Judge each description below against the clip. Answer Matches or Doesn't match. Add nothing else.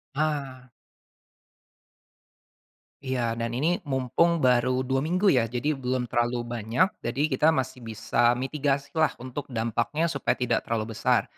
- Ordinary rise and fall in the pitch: Matches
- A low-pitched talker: Matches